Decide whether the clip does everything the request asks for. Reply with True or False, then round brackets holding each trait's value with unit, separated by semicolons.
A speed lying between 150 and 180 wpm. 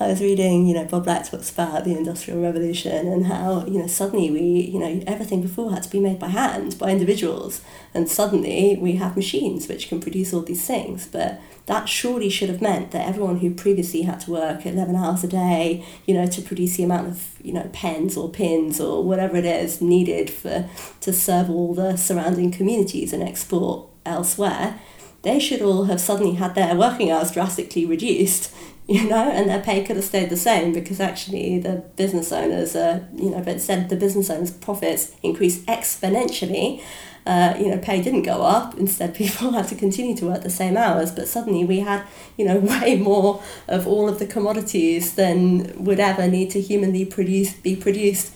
False (200 wpm)